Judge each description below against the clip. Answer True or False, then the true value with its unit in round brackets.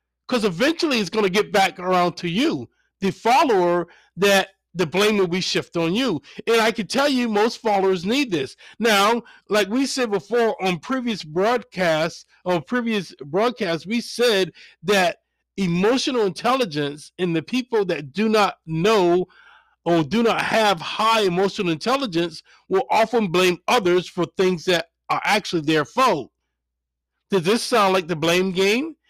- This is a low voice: False (200 Hz)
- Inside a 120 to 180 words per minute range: True (160 wpm)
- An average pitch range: True (4.6 semitones)